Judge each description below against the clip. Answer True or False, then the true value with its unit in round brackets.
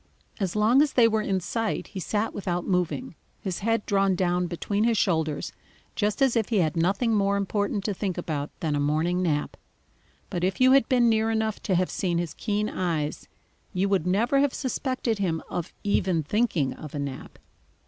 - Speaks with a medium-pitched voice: False (195 Hz)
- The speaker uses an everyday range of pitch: True (4.2 semitones)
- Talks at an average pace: True (195 wpm)